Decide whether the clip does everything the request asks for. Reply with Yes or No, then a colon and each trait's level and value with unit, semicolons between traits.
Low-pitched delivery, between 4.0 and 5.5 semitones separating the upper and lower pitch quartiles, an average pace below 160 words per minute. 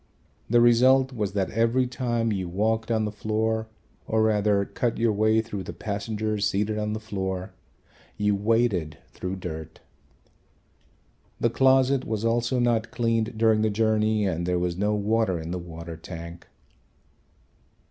No: low, 110 Hz; average, 3.0 semitones; average, 150 wpm